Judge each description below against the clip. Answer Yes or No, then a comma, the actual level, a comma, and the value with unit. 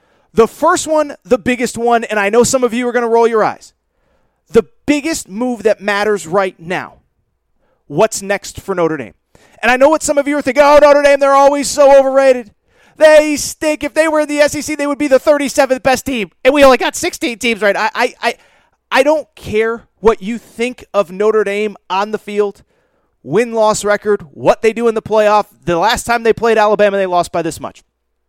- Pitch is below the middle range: No, high, 230 Hz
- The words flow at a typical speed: No, fast, 220 wpm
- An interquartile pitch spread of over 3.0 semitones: Yes, average, 5.3 semitones